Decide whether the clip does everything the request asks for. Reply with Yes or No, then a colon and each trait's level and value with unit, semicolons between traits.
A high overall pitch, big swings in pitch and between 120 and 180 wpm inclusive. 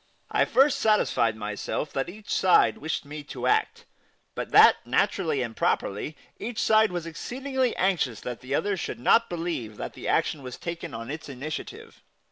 No: medium, 160 Hz; wide, 8.5 semitones; average, 170 wpm